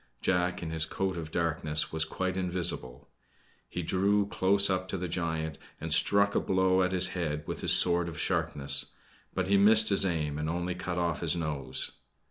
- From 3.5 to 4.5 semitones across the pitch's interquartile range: No, average, 2.7 semitones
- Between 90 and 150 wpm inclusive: No, average, 190 wpm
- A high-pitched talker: No, very low, 90 Hz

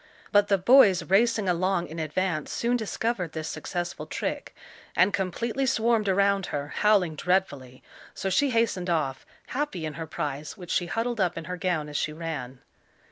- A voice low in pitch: No, medium, 185 Hz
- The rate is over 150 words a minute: Yes, average, 170 wpm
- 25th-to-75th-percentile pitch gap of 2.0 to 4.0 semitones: No, average, 4.8 semitones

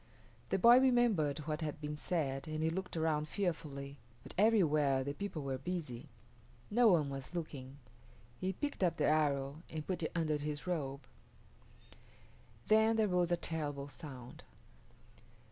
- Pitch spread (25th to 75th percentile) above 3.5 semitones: Yes, average, 4.2 semitones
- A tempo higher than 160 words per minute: No, average, 150 wpm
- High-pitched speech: No, medium, 155 Hz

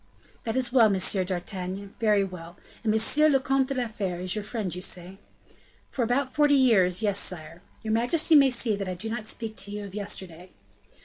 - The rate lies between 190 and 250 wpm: Yes, fast, 205 wpm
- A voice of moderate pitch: No, high, 210 Hz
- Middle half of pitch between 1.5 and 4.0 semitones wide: No, average, 4.7 semitones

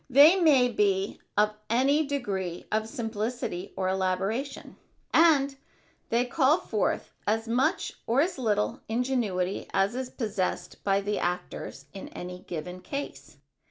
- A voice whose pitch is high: Yes, high, 220 Hz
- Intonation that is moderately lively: No, wide, 5.7 semitones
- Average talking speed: No, slow, 130 wpm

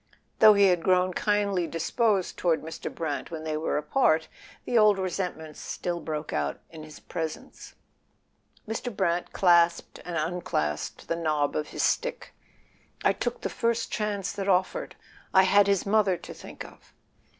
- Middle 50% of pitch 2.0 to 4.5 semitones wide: Yes, average, 4.1 semitones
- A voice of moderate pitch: Yes, medium, 180 Hz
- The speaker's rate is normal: Yes, average, 160 wpm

